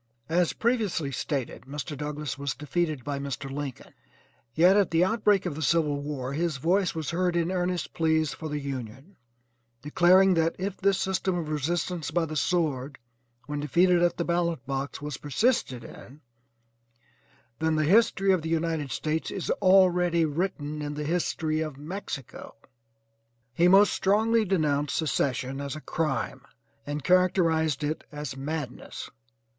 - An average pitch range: Yes, average, 3.6 semitones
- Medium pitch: Yes, medium, 160 Hz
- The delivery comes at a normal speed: Yes, average, 150 wpm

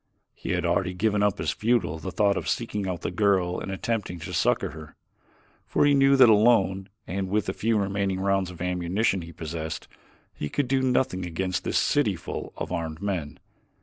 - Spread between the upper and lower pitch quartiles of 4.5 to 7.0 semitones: No, average, 3.3 semitones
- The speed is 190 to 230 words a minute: Yes, average, 195 wpm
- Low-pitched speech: Yes, very low, 95 Hz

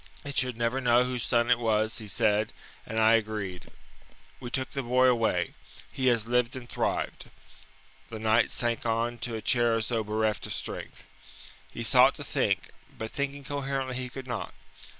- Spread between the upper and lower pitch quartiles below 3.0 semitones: Yes, narrow, 2.4 semitones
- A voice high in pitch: No, low, 120 Hz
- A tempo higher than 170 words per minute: Yes, average, 180 wpm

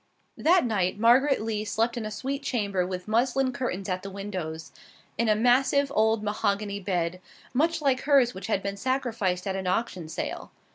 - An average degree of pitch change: Yes, average, 4.9 semitones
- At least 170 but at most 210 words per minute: Yes, average, 180 wpm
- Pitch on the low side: No, high, 215 Hz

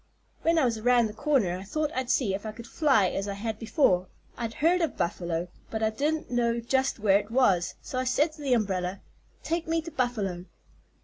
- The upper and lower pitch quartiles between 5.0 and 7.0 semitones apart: Yes, wide, 5.5 semitones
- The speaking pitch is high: Yes, high, 235 Hz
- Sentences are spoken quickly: Yes, fast, 220 wpm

